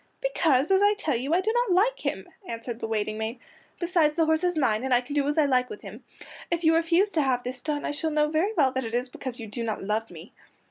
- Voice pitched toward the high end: Yes, very high, 290 Hz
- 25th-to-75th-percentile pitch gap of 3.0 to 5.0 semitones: No, wide, 5.5 semitones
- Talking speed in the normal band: No, fast, 275 wpm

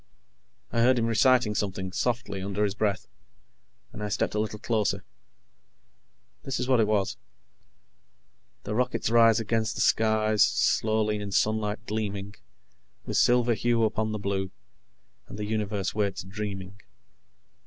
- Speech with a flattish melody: Yes, narrow, 2.0 semitones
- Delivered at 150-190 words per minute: No, average, 140 wpm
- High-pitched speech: No, low, 105 Hz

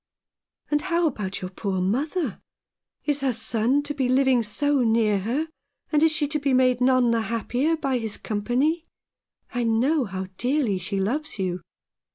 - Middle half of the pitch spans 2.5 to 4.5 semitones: No, average, 5.1 semitones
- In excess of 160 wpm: Yes, average, 170 wpm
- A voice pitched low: No, very high, 250 Hz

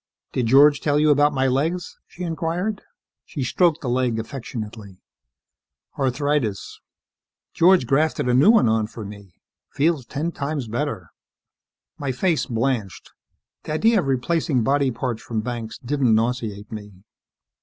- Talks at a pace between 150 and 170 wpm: No, average, 140 wpm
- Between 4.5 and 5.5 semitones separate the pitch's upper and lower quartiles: Yes, average, 4.8 semitones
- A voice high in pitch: No, low, 130 Hz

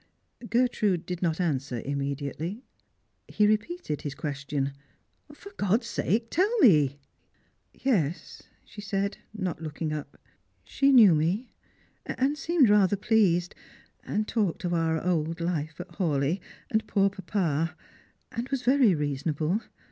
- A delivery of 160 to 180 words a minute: No, average, 140 wpm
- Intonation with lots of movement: Yes, wide, 6.0 semitones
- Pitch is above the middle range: No, medium, 180 Hz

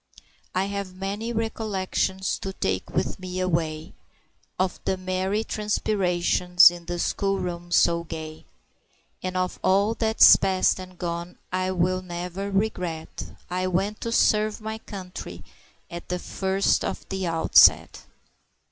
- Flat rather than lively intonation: Yes, narrow, 2.0 semitones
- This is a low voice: No, medium, 185 Hz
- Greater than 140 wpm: No, slow, 135 wpm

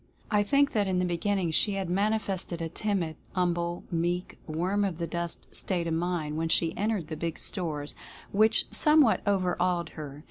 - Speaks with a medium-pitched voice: Yes, medium, 175 Hz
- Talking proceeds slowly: No, average, 185 wpm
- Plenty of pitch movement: No, average, 3.4 semitones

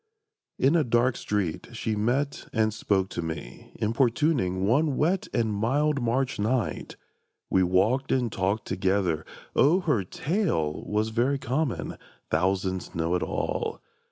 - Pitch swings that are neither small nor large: No, wide, 6.1 semitones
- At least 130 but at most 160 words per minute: Yes, slow, 135 wpm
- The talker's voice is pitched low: Yes, low, 110 Hz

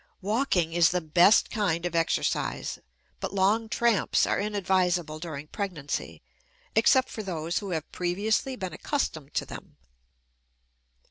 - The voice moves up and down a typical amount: Yes, average, 4.3 semitones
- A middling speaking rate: No, slow, 130 wpm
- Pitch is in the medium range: Yes, medium, 180 Hz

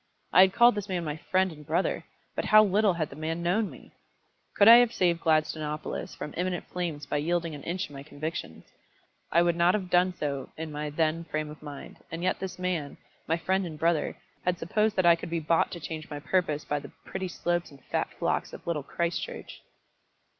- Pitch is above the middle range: No, medium, 170 Hz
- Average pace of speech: No, fast, 220 wpm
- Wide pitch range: No, average, 3.1 semitones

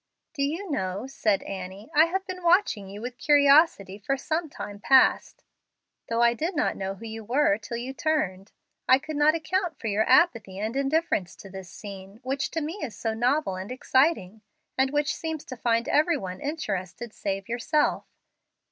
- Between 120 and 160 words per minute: No, average, 185 wpm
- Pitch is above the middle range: Yes, high, 245 Hz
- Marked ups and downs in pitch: Yes, wide, 7.1 semitones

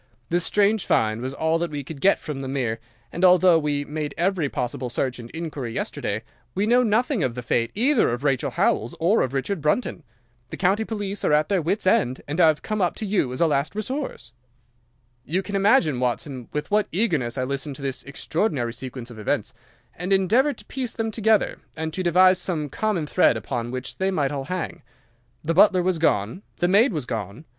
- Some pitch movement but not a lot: No, wide, 6.8 semitones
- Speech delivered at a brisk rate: Yes, fast, 210 wpm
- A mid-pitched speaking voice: Yes, medium, 160 Hz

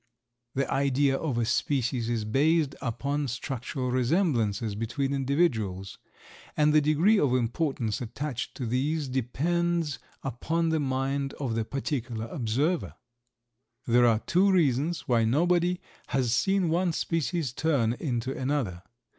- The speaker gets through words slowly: Yes, slow, 130 wpm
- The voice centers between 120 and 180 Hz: Yes, low, 135 Hz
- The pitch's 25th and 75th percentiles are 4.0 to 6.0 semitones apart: Yes, average, 4.8 semitones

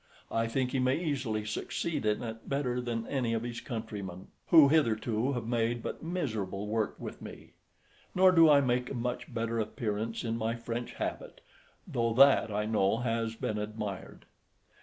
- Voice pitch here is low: Yes, low, 115 Hz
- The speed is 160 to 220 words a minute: Yes, average, 170 wpm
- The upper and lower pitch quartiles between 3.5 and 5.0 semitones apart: No, average, 2.7 semitones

